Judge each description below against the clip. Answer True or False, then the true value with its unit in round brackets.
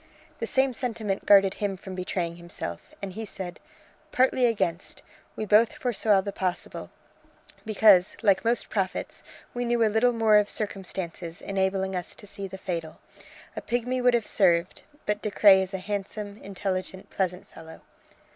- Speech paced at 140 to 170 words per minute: True (160 wpm)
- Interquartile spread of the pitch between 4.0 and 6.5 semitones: False (2.9 semitones)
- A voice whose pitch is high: True (200 Hz)